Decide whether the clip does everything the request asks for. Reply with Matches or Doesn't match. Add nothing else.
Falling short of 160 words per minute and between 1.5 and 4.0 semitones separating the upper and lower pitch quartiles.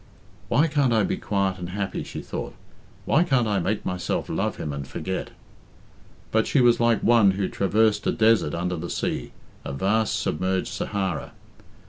Doesn't match